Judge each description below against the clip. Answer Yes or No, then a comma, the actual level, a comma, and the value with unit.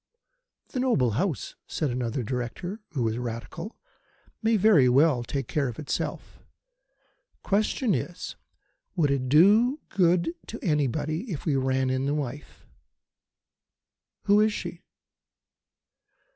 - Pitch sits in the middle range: Yes, medium, 150 Hz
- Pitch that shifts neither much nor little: No, wide, 7.2 semitones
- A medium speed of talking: No, slow, 125 wpm